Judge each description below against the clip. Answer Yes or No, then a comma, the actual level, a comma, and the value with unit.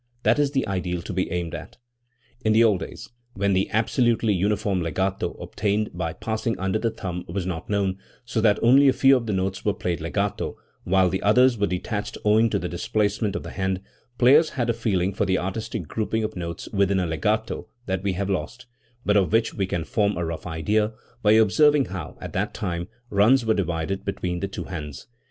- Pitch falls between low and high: No, low, 100 Hz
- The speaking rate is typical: No, fast, 210 wpm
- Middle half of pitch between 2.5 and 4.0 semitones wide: Yes, average, 3.3 semitones